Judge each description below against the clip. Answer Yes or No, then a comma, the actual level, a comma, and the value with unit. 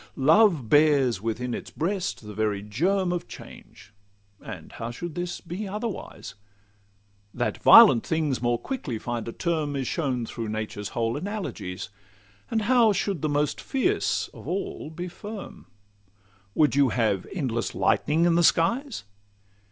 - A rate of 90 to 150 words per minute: Yes, average, 145 wpm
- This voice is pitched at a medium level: Yes, medium, 150 Hz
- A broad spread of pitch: Yes, wide, 8.0 semitones